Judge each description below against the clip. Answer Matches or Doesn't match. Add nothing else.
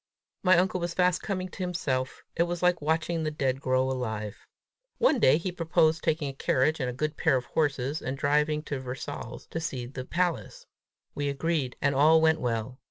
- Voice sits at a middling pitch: Matches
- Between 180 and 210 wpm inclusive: Matches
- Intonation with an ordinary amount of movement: Matches